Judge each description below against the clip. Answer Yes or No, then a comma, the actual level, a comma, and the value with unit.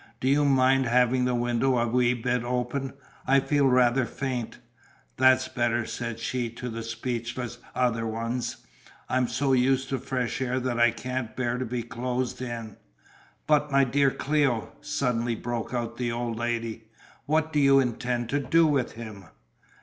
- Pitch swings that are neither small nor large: No, narrow, 2.0 semitones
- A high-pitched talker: No, low, 125 Hz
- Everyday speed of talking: Yes, average, 165 wpm